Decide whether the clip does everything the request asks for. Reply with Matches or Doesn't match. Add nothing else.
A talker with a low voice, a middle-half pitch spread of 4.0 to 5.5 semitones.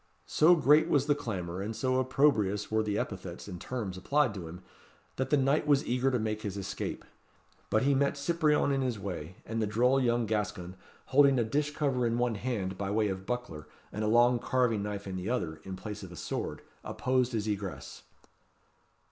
Matches